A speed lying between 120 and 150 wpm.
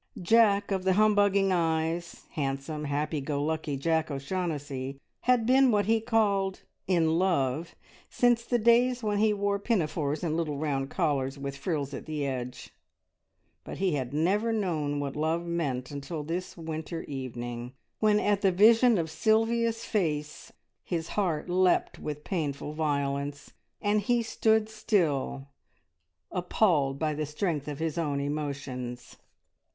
Yes: average, 145 wpm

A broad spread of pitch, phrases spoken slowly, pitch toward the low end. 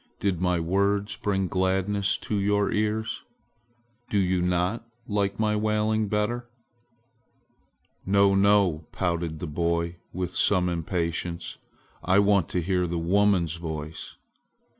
No: average, 3.0 semitones; slow, 120 wpm; very low, 95 Hz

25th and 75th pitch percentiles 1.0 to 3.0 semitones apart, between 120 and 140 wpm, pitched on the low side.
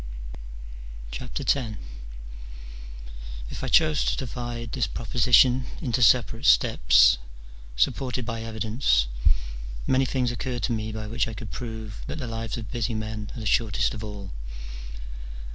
Yes: narrow, 2.6 semitones; slow, 135 wpm; low, 115 Hz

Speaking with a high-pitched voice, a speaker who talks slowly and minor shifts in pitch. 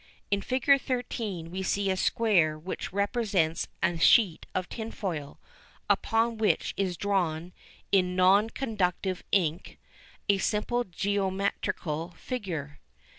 No: high, 195 Hz; slow, 115 wpm; average, 3.7 semitones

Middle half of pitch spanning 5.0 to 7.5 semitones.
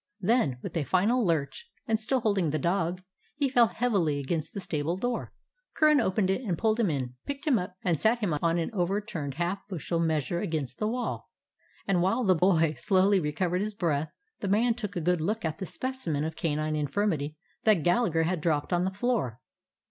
Yes: average, 5.3 semitones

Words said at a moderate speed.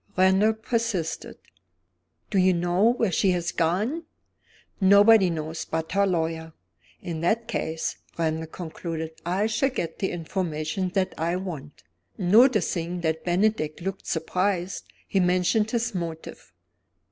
No: slow, 125 wpm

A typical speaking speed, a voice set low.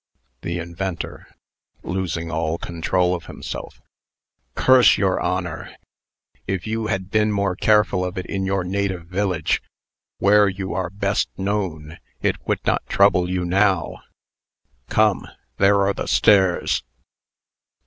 No: slow, 130 wpm; very low, 95 Hz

